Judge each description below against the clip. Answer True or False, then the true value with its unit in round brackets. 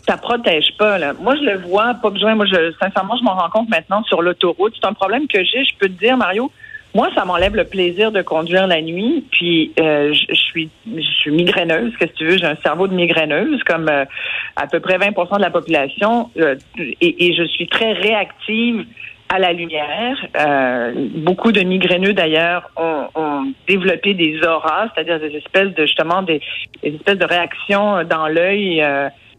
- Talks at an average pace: True (200 wpm)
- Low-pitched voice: False (180 Hz)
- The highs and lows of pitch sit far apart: False (4.4 semitones)